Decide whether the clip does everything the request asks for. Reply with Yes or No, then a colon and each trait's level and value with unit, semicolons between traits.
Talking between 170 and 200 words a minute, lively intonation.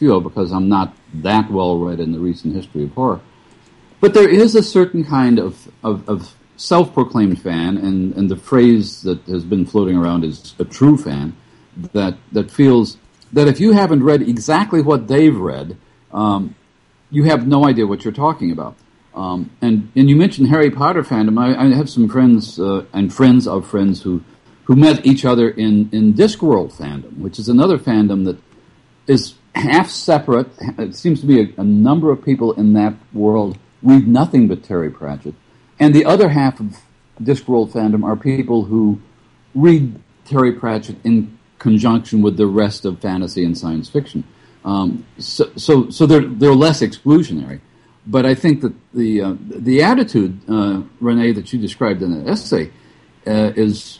Yes: average, 175 wpm; wide, 5.8 semitones